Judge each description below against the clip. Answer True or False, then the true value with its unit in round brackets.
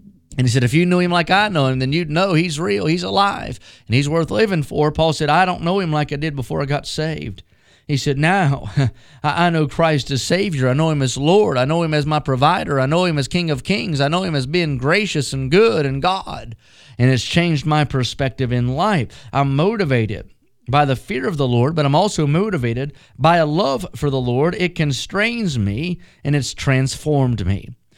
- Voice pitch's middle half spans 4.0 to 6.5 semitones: True (4.5 semitones)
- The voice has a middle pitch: True (150 Hz)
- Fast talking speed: True (225 wpm)